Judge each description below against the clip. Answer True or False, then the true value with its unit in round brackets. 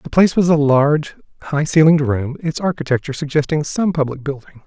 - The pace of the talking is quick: False (180 wpm)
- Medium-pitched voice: True (150 Hz)